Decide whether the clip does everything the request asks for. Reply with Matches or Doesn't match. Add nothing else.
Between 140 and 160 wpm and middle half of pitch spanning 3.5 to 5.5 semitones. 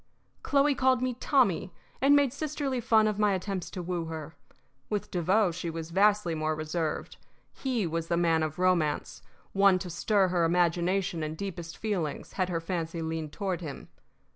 Doesn't match